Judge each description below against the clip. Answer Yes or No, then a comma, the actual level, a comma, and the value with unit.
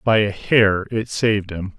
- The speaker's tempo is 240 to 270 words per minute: No, average, 200 wpm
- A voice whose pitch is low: Yes, low, 105 Hz